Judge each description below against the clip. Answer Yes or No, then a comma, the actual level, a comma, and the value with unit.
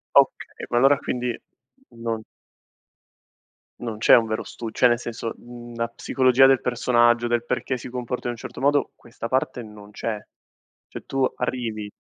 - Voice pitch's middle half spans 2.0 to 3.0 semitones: No, narrow, 1.5 semitones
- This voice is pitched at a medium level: No, low, 120 Hz